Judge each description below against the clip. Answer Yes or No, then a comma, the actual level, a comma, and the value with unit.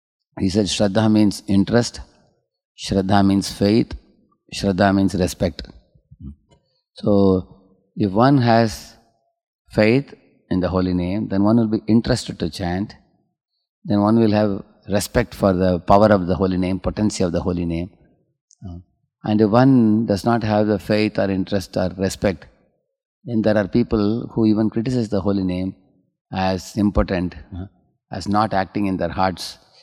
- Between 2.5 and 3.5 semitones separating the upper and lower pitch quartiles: Yes, average, 2.8 semitones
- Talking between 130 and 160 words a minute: Yes, average, 150 wpm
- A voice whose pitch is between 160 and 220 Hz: No, low, 100 Hz